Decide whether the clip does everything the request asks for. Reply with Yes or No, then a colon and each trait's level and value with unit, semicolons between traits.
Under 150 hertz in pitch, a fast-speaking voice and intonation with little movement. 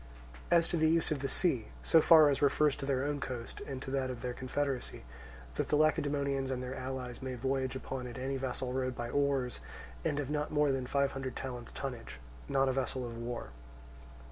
Yes: low, 135 Hz; fast, 215 wpm; narrow, 2.0 semitones